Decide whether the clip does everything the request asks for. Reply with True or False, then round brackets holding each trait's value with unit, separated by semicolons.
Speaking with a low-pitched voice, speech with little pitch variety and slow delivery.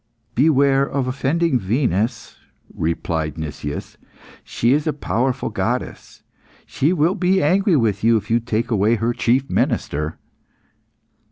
False (120 Hz; 5.1 semitones; 125 wpm)